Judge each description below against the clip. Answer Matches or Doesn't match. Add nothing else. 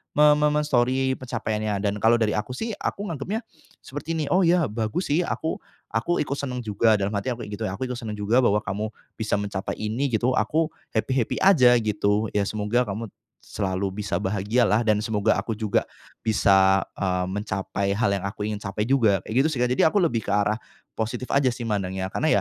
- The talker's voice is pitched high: Doesn't match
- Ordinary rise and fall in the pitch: Matches